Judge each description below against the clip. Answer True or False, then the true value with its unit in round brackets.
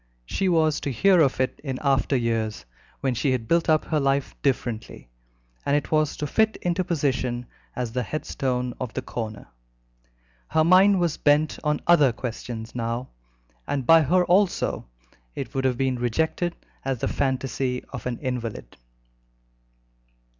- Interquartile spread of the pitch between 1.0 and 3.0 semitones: False (4.2 semitones)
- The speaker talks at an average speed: True (155 wpm)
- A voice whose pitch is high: False (135 Hz)